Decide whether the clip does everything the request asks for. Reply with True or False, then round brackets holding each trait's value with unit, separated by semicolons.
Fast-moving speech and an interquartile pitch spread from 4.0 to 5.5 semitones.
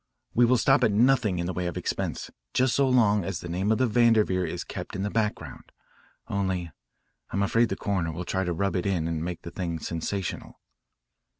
True (210 wpm; 4.4 semitones)